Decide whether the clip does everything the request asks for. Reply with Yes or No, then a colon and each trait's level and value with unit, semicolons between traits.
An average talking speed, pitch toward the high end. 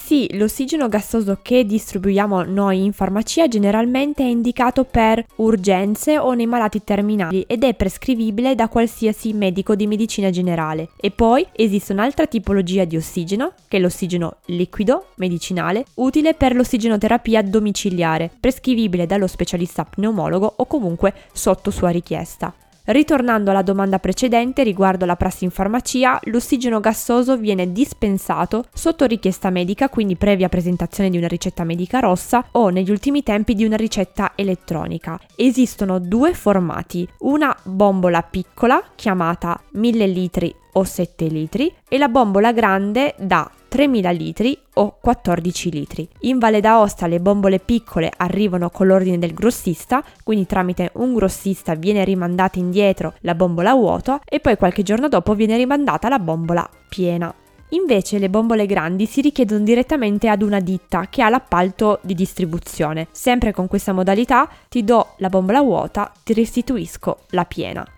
Yes: average, 145 wpm; high, 205 Hz